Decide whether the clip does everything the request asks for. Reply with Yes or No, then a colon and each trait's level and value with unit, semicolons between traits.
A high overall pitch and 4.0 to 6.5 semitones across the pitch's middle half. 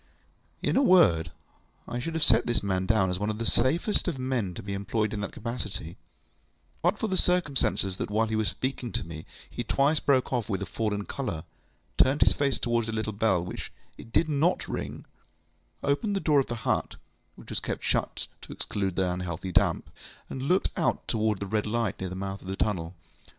No: low, 110 Hz; wide, 5.6 semitones